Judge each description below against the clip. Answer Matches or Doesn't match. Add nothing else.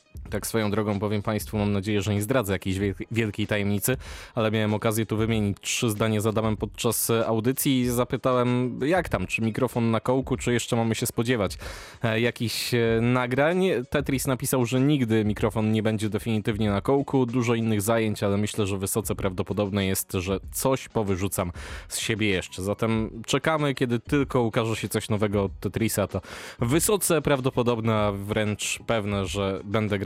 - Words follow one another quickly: Matches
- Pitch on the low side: Matches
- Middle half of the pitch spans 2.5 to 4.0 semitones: Matches